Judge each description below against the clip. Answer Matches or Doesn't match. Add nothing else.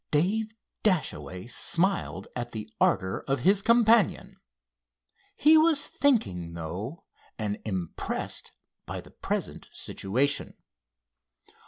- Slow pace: Matches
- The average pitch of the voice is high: Doesn't match